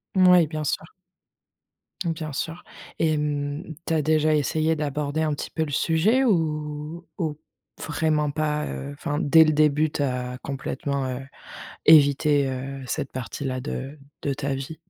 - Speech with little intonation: Yes, narrow, 2.0 semitones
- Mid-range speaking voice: Yes, medium, 150 Hz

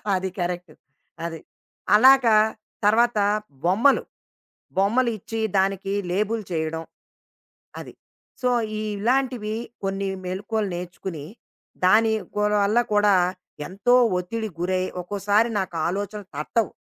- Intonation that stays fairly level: No, average, 3.4 semitones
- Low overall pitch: No, high, 205 Hz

